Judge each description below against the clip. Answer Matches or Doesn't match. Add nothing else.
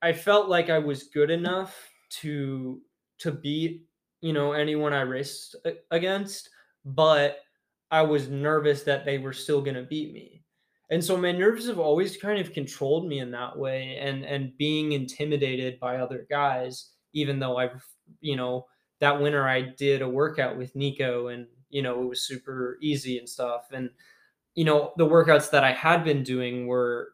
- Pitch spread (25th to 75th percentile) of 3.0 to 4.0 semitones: Matches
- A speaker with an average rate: Matches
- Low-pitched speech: Doesn't match